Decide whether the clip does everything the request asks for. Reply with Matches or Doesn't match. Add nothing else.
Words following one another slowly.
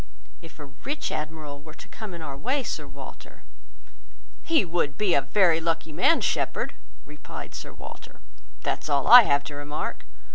Doesn't match